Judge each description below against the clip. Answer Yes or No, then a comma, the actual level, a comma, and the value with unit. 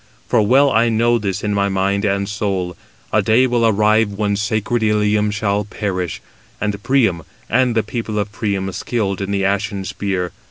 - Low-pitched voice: Yes, low, 105 Hz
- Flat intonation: Yes, narrow, 2.1 semitones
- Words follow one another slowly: No, average, 175 wpm